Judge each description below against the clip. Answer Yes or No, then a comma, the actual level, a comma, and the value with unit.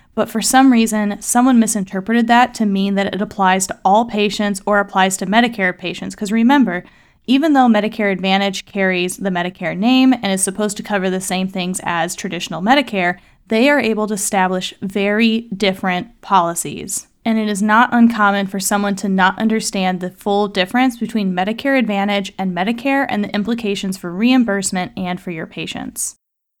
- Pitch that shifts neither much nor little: Yes, average, 3.0 semitones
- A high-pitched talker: Yes, high, 205 Hz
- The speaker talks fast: No, average, 170 wpm